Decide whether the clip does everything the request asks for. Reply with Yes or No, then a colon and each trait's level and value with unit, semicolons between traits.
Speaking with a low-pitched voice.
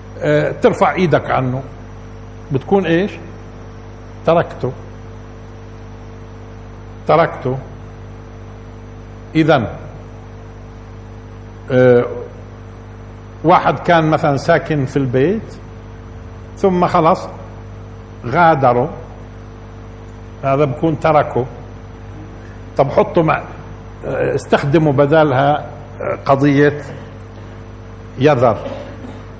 Yes: low, 110 Hz